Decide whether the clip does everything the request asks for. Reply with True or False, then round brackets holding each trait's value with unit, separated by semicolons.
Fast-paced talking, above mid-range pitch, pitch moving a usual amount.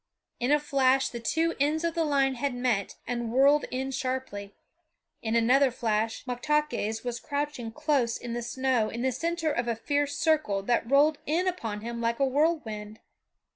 False (175 wpm; 260 Hz; 4.0 semitones)